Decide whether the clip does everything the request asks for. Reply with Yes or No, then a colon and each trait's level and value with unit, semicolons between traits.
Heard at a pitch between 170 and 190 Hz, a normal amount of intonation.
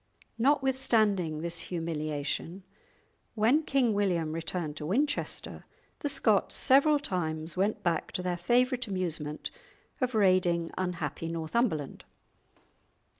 No: medium, 185 Hz; wide, 6.5 semitones